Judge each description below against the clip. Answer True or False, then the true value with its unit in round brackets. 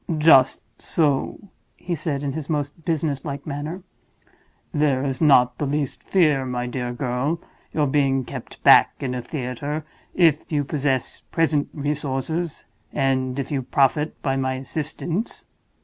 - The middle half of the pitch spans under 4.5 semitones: True (2.6 semitones)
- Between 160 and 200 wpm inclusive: False (150 wpm)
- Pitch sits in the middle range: True (145 Hz)